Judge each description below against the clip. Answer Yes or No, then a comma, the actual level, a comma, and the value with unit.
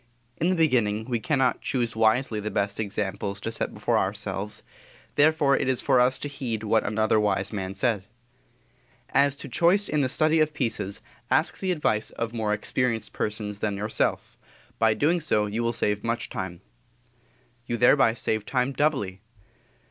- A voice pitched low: Yes, low, 115 Hz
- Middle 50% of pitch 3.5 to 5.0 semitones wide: Yes, average, 4.7 semitones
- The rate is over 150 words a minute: Yes, average, 170 wpm